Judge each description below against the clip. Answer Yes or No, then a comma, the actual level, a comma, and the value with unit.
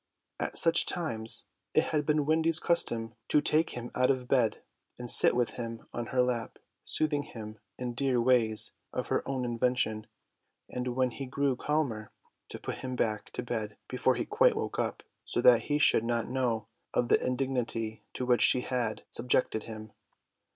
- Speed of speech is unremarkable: Yes, average, 180 wpm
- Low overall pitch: Yes, low, 125 Hz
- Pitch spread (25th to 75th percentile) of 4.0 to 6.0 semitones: No, average, 3.2 semitones